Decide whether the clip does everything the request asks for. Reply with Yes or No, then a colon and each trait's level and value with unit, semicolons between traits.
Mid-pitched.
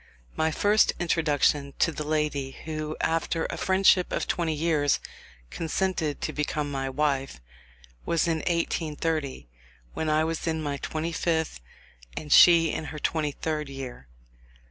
Yes: medium, 155 Hz